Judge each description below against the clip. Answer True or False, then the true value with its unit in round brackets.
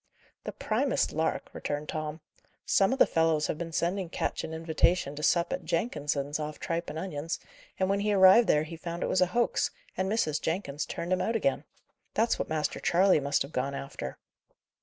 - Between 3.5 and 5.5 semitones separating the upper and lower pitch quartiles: True (3.8 semitones)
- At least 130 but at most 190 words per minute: False (200 wpm)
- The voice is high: False (165 Hz)